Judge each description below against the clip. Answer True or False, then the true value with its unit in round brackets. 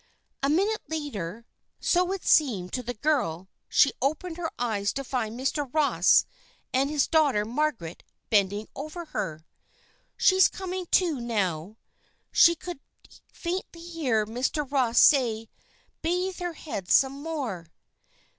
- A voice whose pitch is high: True (275 Hz)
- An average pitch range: False (6.9 semitones)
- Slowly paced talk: True (130 wpm)